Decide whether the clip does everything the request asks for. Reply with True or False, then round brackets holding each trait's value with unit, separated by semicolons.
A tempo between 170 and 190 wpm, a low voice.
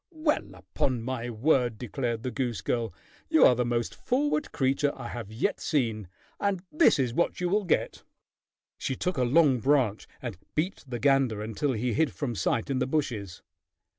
True (180 wpm; 130 Hz)